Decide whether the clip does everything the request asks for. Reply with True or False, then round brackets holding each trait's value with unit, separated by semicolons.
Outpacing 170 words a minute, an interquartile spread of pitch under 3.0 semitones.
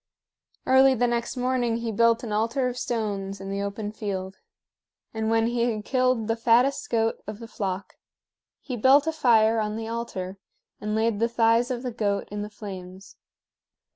True (180 wpm; 2.6 semitones)